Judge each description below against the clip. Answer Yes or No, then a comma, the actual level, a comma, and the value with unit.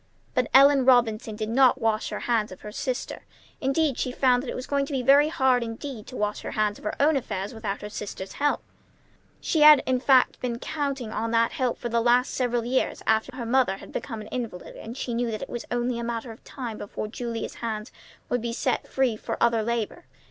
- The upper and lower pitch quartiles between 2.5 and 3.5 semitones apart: Yes, average, 2.8 semitones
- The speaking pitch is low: No, high, 240 Hz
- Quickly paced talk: Yes, fast, 225 wpm